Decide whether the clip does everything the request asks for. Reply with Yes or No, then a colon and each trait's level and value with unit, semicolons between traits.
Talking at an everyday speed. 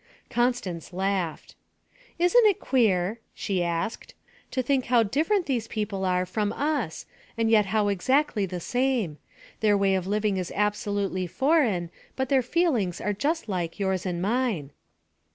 Yes: average, 150 wpm